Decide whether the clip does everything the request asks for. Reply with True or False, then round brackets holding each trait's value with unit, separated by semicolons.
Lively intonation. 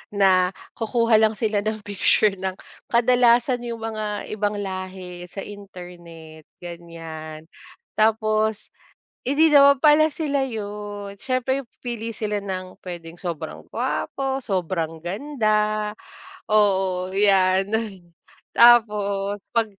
False (3.6 semitones)